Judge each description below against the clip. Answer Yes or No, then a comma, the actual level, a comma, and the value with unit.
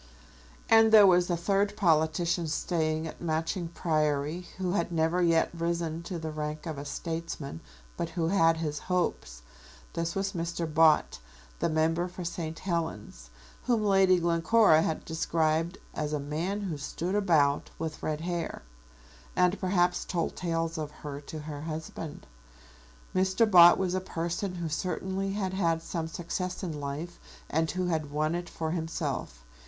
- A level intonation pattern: Yes, narrow, 2.3 semitones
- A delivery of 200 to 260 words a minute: No, average, 160 wpm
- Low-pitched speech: No, medium, 165 Hz